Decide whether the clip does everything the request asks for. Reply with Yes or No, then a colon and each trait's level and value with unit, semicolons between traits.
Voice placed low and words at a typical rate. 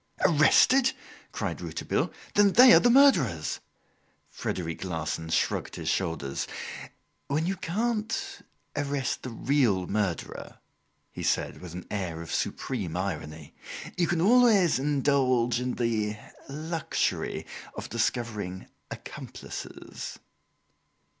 No: low, 125 Hz; slow, 110 wpm